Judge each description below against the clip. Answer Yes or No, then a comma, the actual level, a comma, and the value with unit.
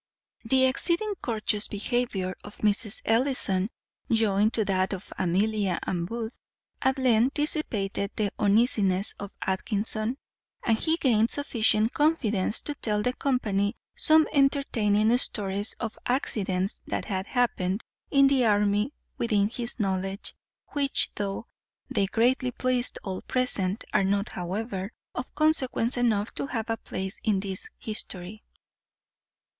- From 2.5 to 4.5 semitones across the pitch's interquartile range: Yes, average, 4.0 semitones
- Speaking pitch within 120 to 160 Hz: No, high, 215 Hz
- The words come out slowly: Yes, slow, 130 wpm